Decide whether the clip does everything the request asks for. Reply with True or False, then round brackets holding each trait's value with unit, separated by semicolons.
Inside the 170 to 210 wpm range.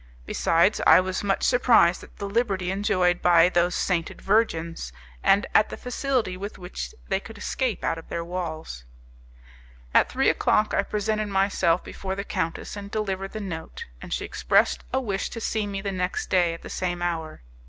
True (185 wpm)